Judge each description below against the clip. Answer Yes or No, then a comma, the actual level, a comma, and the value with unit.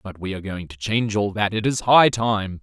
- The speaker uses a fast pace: Yes, fast, 275 wpm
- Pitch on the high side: No, low, 105 Hz